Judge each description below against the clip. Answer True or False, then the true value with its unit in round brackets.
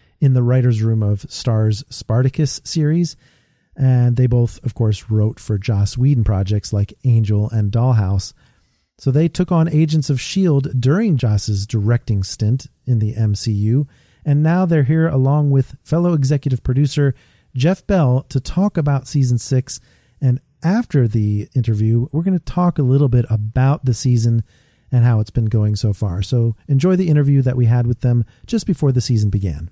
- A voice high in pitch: False (125 Hz)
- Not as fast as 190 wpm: True (175 wpm)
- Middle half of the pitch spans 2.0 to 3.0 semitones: False (4.3 semitones)